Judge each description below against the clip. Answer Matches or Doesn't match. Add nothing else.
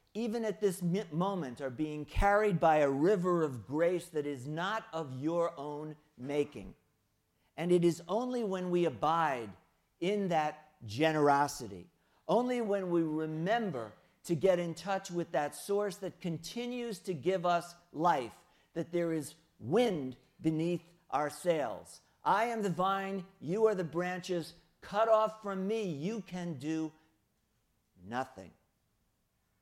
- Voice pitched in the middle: Matches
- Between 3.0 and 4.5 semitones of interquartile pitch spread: Matches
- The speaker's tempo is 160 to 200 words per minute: Doesn't match